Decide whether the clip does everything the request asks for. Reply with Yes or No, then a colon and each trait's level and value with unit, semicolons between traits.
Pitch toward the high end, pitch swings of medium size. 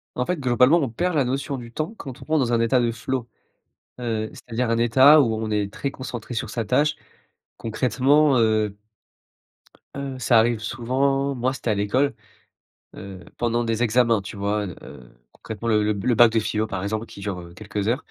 No: low, 115 Hz; average, 3.3 semitones